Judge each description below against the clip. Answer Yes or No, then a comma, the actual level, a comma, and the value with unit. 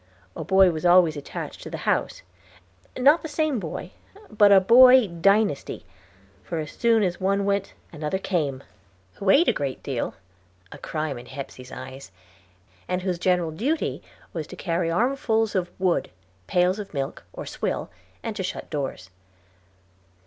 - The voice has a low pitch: No, medium, 185 Hz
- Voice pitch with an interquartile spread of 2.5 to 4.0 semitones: No, wide, 5.6 semitones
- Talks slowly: No, average, 155 wpm